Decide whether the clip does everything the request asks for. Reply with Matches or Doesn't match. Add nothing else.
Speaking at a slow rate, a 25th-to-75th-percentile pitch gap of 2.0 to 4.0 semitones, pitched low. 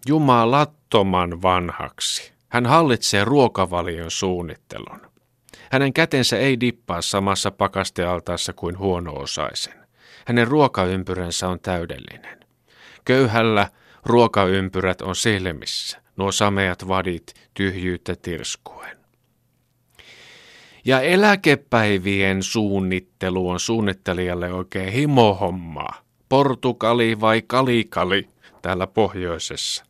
Doesn't match